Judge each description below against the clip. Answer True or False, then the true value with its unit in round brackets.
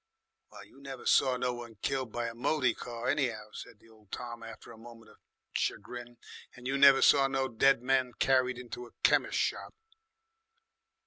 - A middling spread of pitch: False (2.3 semitones)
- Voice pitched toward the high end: False (125 Hz)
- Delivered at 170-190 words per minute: True (175 wpm)